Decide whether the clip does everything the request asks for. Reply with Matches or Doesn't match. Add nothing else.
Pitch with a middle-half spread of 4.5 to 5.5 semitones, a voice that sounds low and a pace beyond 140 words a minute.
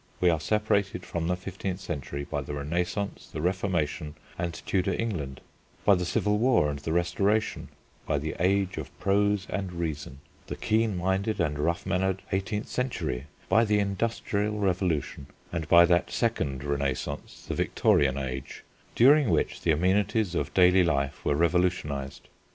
Matches